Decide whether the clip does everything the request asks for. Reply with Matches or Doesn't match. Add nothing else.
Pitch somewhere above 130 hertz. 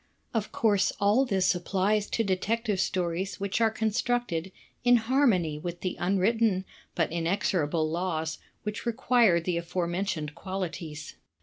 Matches